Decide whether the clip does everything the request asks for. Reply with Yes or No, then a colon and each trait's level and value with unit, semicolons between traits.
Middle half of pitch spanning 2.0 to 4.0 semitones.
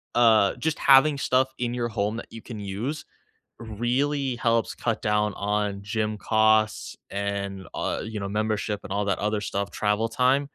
Yes: average, 2.9 semitones